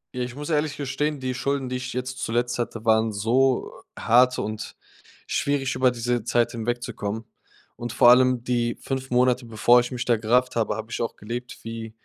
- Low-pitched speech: Yes, low, 125 Hz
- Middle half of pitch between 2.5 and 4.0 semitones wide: No, narrow, 1.9 semitones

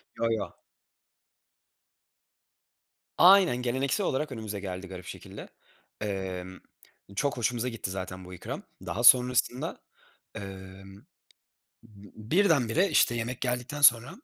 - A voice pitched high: No, low, 115 Hz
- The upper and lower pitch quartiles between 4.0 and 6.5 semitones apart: Yes, average, 4.8 semitones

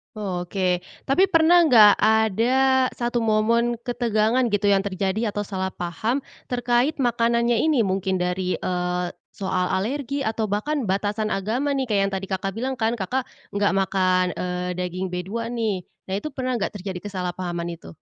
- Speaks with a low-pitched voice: No, high, 210 Hz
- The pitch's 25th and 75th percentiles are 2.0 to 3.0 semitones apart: No, average, 4.2 semitones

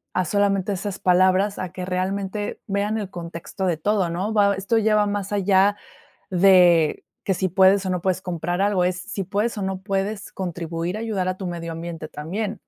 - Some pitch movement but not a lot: No, narrow, 2.1 semitones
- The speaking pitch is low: No, high, 190 Hz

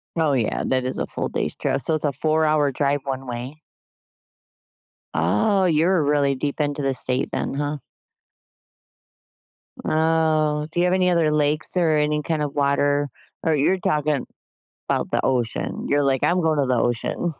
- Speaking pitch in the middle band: Yes, medium, 150 Hz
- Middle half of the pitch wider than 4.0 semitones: No, narrow, 2.4 semitones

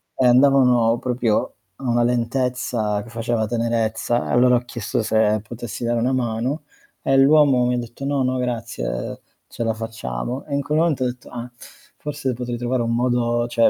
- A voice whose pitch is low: Yes, low, 120 Hz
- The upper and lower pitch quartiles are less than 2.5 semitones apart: Yes, narrow, 1.8 semitones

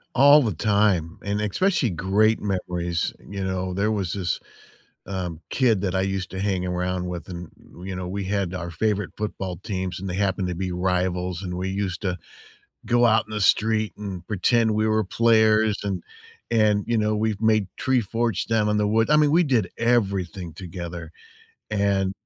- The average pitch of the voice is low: Yes, low, 100 Hz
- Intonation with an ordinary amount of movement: Yes, average, 3.0 semitones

